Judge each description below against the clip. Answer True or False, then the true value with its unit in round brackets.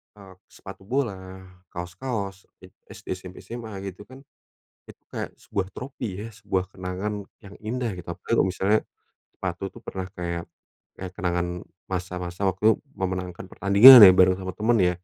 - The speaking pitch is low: True (95 Hz)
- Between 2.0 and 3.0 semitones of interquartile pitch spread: True (2.5 semitones)